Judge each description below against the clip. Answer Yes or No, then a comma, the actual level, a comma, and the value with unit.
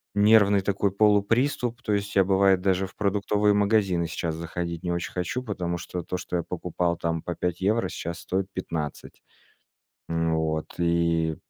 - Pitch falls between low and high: No, very low, 95 Hz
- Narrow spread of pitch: No, average, 3.2 semitones